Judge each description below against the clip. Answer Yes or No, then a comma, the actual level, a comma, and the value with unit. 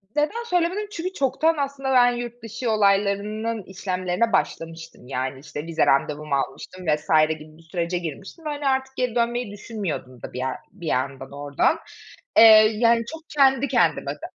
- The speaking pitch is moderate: No, high, 210 Hz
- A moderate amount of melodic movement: No, wide, 9.0 semitones